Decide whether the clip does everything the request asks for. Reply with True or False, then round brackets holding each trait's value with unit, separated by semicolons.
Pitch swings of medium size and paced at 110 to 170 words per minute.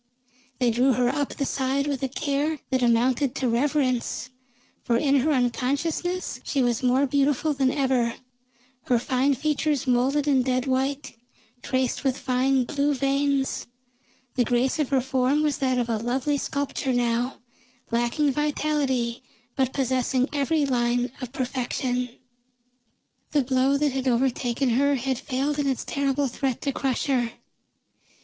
False (2.2 semitones; 150 wpm)